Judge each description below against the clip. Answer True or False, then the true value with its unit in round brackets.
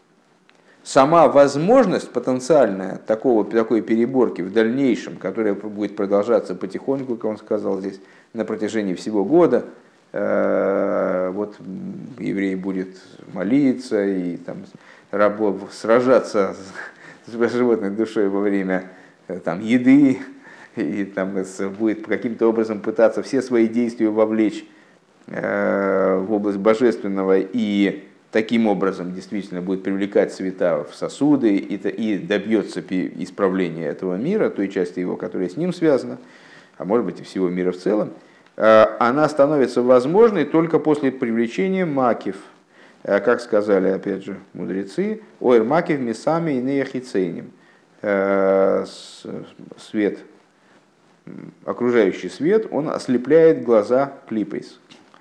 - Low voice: True (110 Hz)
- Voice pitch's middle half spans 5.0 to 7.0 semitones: True (5.3 semitones)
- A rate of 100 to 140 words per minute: True (110 wpm)